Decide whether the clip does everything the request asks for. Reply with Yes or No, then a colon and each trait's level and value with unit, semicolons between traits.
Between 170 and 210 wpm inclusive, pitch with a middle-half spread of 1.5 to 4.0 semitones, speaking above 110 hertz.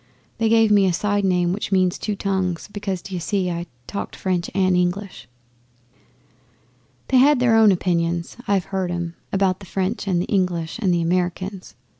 Yes: average, 175 wpm; narrow, 2.4 semitones; medium, 185 Hz